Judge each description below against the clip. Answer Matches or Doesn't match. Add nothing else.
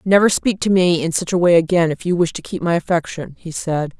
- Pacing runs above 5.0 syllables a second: Matches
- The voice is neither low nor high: Matches